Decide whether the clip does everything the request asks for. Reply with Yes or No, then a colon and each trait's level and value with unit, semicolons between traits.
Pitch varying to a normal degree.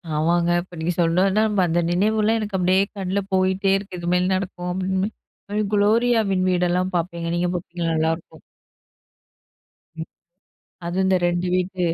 No: narrow, 1.9 semitones